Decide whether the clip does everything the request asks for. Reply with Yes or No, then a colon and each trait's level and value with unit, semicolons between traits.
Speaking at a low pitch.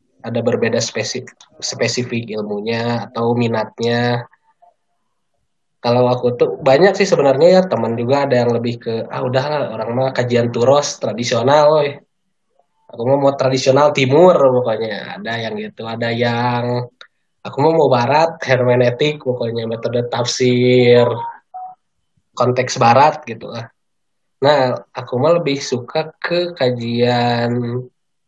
Yes: low, 125 Hz